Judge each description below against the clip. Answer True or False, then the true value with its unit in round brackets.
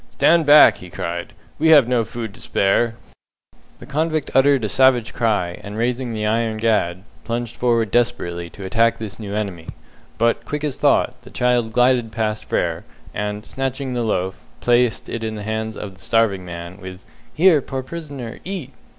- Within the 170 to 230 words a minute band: True (175 wpm)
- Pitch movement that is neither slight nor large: True (3.7 semitones)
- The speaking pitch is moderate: False (115 Hz)